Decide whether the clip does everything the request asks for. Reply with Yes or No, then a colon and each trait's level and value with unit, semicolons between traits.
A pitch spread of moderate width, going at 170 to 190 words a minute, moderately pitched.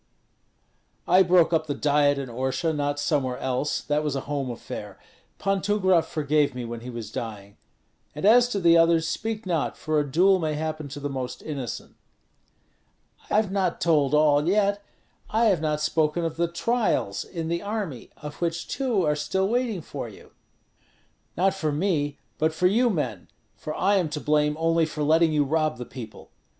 Yes: average, 4.2 semitones; average, 185 wpm; medium, 155 Hz